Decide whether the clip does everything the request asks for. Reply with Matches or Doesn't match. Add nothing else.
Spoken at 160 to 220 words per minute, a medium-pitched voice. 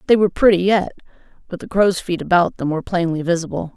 Matches